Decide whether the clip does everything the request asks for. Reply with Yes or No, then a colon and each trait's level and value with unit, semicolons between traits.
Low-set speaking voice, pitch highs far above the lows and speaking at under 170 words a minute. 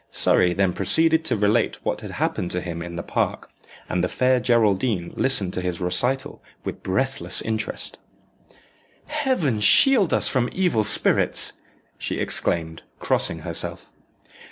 Yes: low, 110 Hz; wide, 7.0 semitones; average, 140 wpm